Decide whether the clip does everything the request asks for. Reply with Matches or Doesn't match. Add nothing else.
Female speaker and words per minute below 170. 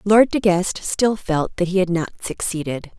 Doesn't match